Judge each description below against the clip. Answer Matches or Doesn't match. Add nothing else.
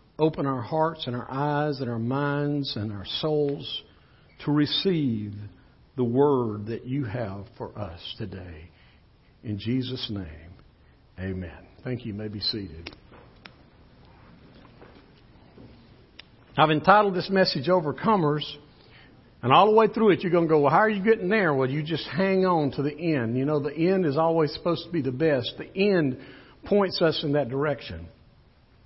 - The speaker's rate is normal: Matches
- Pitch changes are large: Matches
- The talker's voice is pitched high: Doesn't match